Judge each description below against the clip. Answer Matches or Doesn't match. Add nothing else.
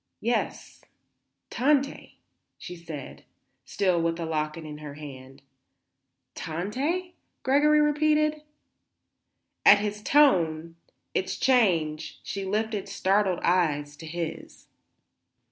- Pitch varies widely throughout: Matches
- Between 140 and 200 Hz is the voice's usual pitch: Matches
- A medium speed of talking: Doesn't match